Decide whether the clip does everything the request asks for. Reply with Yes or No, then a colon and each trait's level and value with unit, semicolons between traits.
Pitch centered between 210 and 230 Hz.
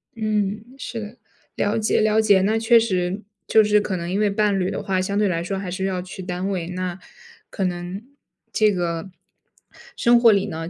No: high, 195 Hz